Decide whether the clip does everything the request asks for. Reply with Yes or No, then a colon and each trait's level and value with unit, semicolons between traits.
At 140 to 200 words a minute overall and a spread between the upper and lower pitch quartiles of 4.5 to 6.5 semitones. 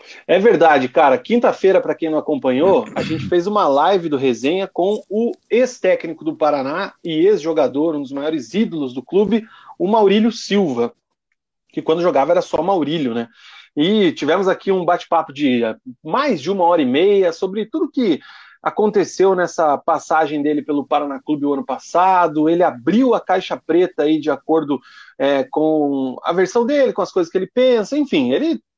Yes: average, 175 wpm; wide, 5.6 semitones